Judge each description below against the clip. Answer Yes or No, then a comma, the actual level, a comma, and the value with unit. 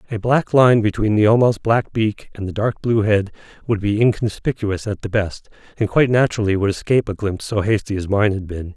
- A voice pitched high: No, low, 105 Hz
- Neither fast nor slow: No, fast, 220 wpm